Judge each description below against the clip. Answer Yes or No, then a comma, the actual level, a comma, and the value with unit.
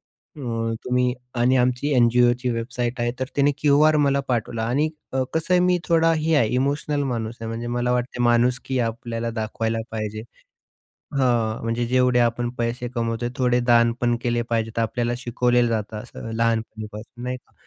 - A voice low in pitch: Yes, low, 120 Hz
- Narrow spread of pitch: Yes, narrow, 1.7 semitones